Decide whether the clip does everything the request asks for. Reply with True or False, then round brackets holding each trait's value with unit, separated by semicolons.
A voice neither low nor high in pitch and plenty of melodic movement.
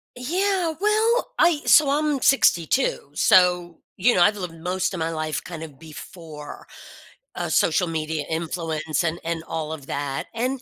True (175 Hz; 8.9 semitones)